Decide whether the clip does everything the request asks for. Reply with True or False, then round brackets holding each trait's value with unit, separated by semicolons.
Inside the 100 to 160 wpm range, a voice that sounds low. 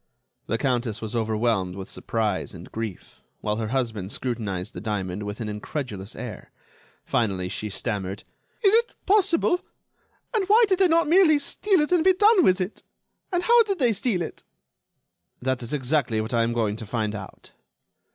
False (175 wpm; 120 Hz)